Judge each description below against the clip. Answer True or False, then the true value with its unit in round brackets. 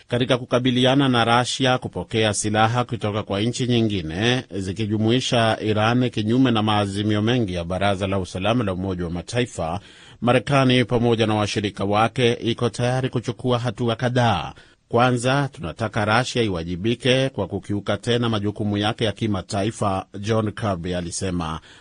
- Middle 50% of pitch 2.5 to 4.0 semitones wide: True (3.4 semitones)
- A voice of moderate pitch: False (110 Hz)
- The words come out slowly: False (130 wpm)